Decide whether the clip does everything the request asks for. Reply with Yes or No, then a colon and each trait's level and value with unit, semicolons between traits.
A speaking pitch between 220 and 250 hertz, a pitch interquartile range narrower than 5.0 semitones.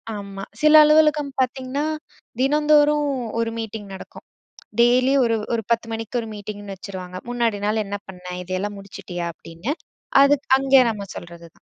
No: high, 225 Hz; wide, 5.5 semitones